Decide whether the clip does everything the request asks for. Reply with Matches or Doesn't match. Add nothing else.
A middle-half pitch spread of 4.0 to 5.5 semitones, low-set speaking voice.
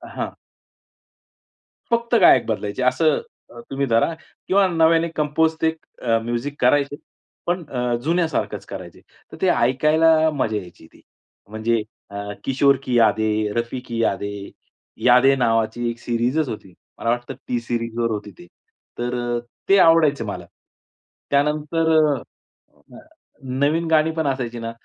Matches